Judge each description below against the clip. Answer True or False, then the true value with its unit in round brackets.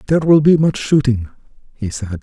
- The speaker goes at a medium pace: True (190 wpm)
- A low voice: True (130 Hz)